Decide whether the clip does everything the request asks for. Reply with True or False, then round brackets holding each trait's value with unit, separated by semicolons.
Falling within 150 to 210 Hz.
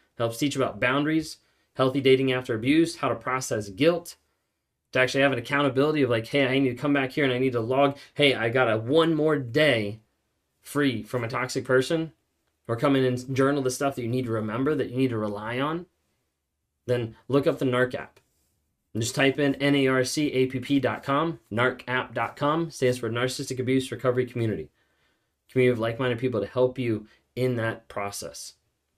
False (130 Hz)